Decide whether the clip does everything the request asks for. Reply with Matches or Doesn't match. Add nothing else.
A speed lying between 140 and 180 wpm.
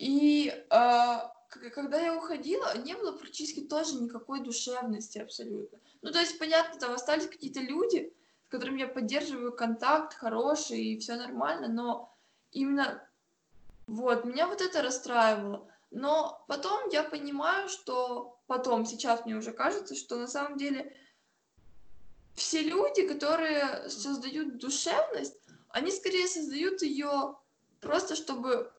Doesn't match